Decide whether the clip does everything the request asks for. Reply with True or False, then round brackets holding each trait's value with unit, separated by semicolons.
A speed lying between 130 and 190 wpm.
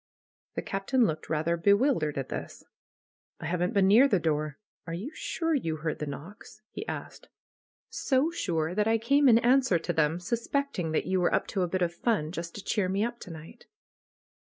False (200 wpm)